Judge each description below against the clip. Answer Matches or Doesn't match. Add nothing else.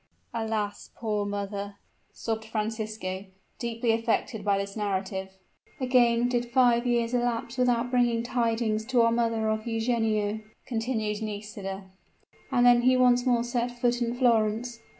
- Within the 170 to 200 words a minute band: Doesn't match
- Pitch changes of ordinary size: Doesn't match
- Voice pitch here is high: Matches